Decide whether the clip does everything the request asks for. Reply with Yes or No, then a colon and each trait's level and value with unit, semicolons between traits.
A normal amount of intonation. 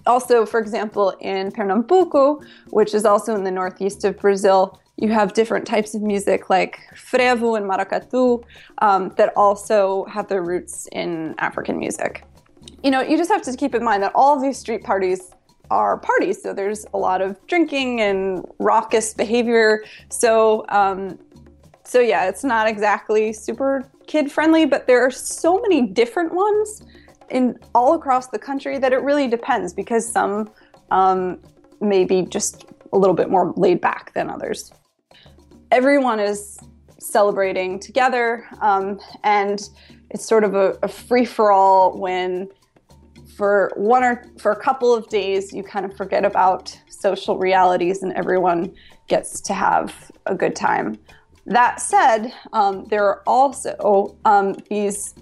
Yes: average, 4.4 semitones